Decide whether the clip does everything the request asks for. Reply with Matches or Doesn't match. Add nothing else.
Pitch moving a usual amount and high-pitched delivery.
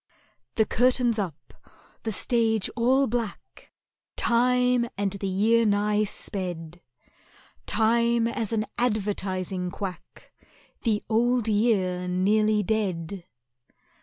Matches